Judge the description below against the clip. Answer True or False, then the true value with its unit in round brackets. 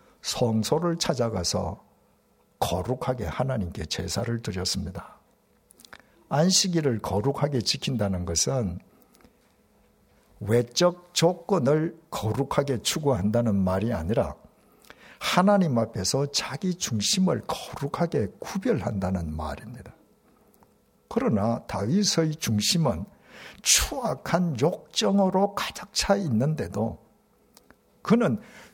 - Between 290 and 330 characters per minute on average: False (220 characters per minute)